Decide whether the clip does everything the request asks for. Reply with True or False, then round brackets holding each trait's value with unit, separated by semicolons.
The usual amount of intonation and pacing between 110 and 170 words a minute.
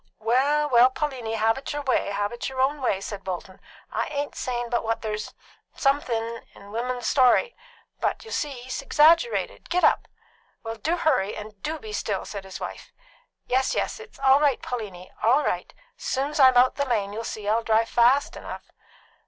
False (4.4 semitones; 190 wpm)